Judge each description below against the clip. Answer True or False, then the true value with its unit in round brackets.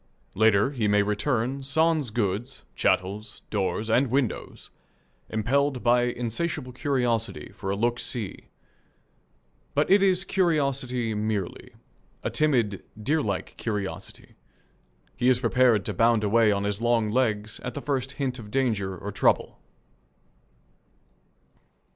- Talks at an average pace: False (125 wpm)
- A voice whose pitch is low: True (120 Hz)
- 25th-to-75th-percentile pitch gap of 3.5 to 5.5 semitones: True (4.2 semitones)